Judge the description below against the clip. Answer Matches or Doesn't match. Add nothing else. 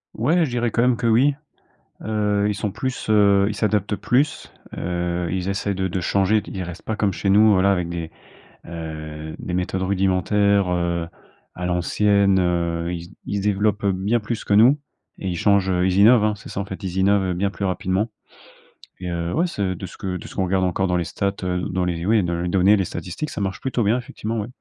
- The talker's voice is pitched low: Matches